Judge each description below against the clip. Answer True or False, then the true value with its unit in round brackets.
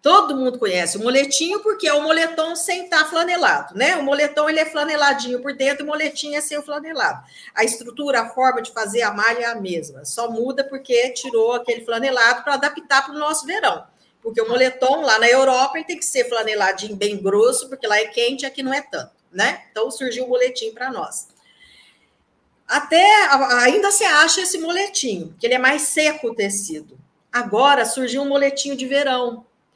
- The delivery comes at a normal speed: False (195 wpm)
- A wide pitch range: False (4.2 semitones)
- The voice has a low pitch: False (270 Hz)